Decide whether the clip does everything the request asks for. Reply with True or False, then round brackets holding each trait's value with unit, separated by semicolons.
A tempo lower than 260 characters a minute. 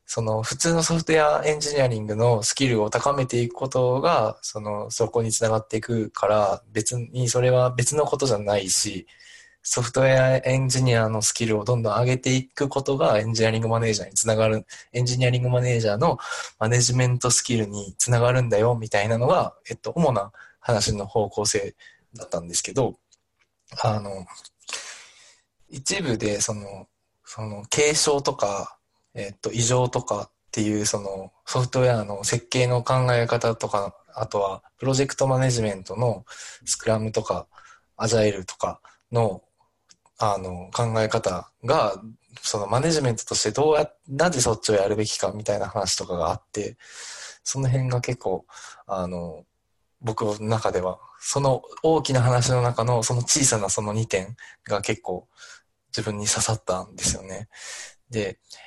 False (330 characters per minute)